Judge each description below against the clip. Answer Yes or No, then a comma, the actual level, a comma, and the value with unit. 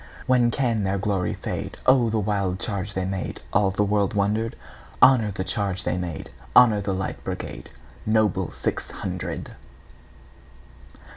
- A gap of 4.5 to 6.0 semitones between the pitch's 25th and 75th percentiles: No, average, 2.7 semitones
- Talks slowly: Yes, slow, 120 wpm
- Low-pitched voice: Yes, low, 100 Hz